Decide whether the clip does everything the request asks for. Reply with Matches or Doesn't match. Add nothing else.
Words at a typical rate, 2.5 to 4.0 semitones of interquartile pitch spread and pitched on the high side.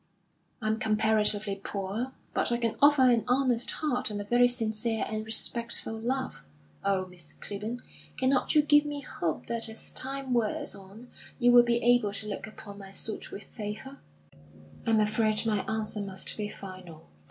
Matches